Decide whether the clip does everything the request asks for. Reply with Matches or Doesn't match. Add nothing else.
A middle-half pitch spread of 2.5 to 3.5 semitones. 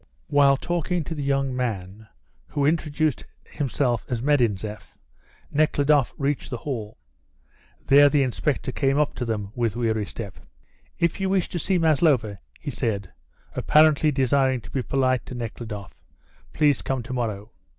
Doesn't match